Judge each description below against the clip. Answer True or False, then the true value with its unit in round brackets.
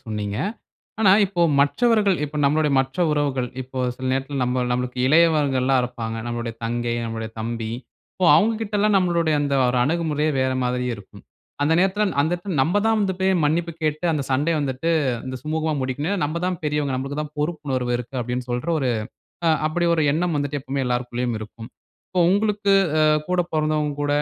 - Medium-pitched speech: True (145 Hz)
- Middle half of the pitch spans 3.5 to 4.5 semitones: False (5.1 semitones)